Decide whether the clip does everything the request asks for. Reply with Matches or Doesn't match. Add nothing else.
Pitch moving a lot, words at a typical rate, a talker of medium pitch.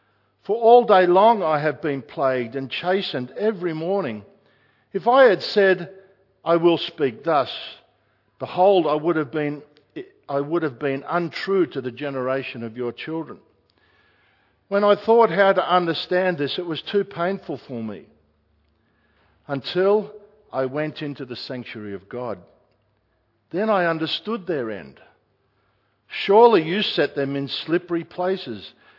Matches